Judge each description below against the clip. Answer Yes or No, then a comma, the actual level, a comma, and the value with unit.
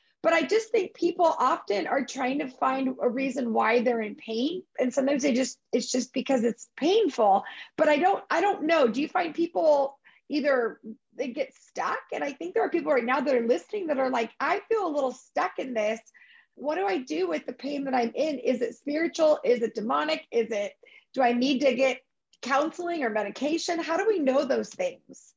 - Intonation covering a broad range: No, average, 4.8 semitones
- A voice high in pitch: Yes, very high, 275 Hz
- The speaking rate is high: Yes, fast, 220 wpm